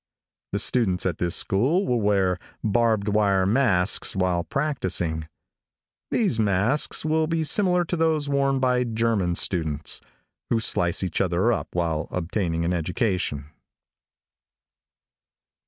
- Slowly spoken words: Yes, slow, 120 wpm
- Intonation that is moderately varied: No, wide, 6.7 semitones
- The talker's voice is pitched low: Yes, low, 100 Hz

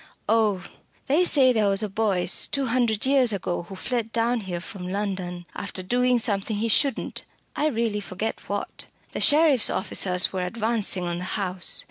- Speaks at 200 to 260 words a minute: No, average, 170 wpm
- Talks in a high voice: Yes, high, 210 Hz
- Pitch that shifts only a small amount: No, average, 4.2 semitones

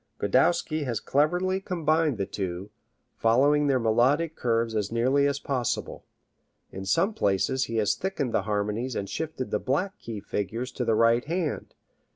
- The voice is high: No, low, 125 Hz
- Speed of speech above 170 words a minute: No, average, 165 wpm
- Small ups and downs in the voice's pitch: No, wide, 5.6 semitones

